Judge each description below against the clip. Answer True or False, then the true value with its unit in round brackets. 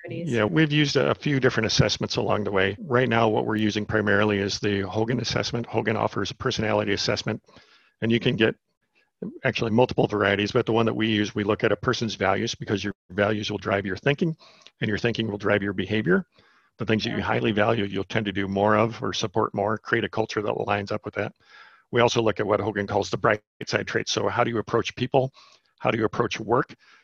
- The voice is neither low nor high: False (110 Hz)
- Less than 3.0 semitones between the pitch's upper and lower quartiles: True (2.6 semitones)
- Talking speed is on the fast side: True (230 wpm)